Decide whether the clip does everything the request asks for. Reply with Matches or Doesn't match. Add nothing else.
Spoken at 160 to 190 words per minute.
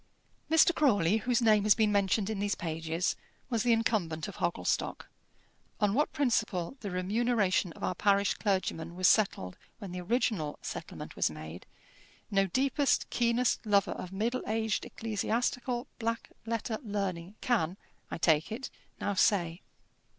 Doesn't match